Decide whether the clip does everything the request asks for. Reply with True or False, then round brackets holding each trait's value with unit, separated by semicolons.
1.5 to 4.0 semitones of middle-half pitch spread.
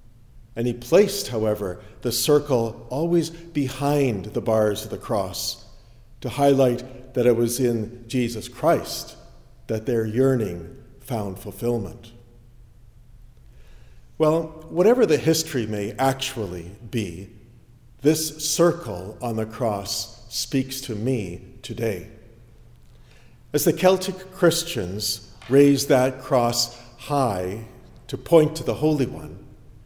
True (3.3 semitones)